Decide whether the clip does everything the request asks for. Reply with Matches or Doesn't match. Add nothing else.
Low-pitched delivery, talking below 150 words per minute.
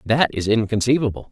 Matches